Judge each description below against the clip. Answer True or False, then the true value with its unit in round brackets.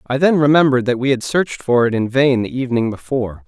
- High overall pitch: False (130 Hz)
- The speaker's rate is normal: False (240 wpm)